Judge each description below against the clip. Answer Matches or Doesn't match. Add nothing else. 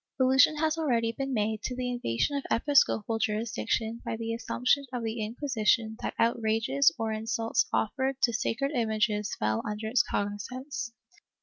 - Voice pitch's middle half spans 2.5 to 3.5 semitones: Matches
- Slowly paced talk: Doesn't match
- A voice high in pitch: Matches